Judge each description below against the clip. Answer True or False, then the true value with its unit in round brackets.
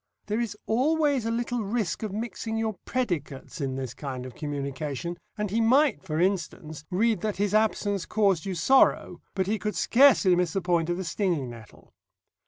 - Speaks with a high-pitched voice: True (195 Hz)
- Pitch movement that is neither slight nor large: False (5.7 semitones)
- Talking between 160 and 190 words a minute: True (185 wpm)